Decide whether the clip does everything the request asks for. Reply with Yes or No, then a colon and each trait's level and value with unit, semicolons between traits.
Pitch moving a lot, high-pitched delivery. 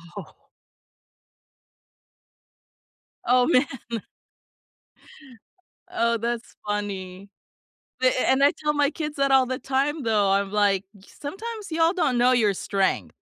Yes: wide, 6.0 semitones; very high, 250 Hz